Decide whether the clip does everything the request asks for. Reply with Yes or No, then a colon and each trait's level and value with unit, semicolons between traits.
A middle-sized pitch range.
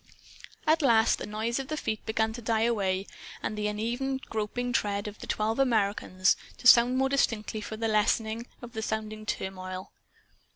No: narrow, 2.2 semitones